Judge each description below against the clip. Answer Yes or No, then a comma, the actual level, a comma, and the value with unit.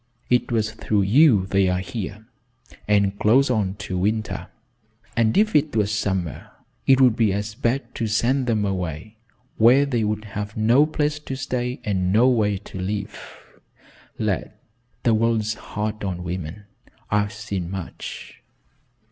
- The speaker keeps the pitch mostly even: No, average, 3.3 semitones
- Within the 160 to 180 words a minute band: No, average, 150 wpm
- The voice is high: No, low, 105 Hz